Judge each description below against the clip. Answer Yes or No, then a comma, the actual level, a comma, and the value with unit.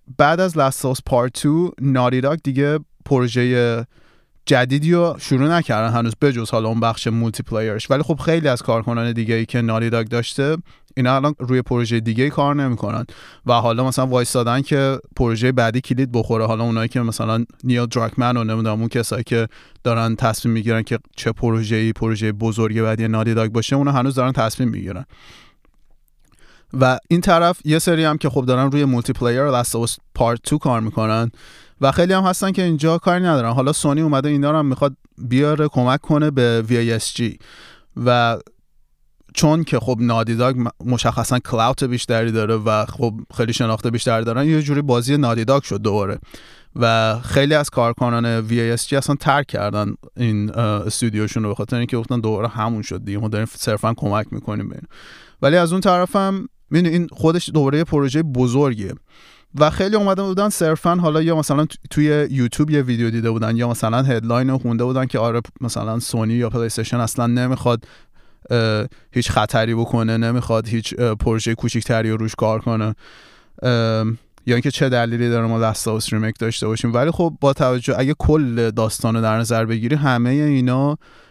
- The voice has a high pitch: No, low, 120 Hz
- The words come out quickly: Yes, fast, 175 wpm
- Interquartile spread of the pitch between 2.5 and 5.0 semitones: Yes, average, 3.5 semitones